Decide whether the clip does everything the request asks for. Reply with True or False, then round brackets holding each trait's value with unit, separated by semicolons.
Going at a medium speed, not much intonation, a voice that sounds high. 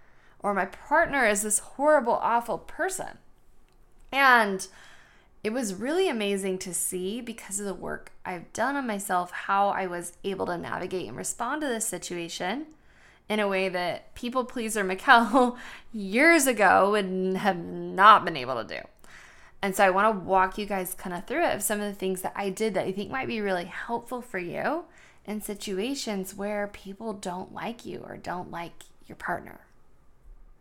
False (180 wpm; 4.3 semitones; 205 Hz)